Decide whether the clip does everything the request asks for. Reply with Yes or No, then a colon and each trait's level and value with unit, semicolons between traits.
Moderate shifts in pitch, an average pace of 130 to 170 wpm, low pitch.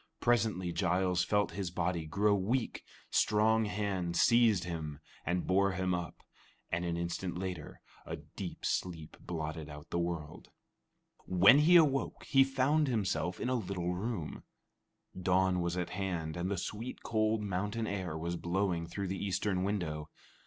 Yes: average, 3.3 semitones; average, 150 wpm; very low, 95 Hz